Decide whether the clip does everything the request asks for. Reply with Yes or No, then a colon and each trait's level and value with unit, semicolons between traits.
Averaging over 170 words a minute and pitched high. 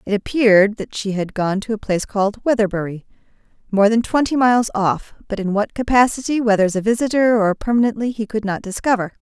Yes: average, 190 wpm; high, 215 Hz